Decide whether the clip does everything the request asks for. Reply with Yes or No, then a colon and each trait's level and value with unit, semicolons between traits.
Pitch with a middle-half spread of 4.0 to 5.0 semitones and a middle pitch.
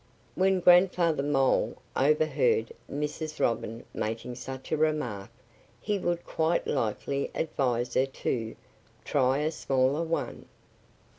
Yes: average, 4.4 semitones; medium, 145 Hz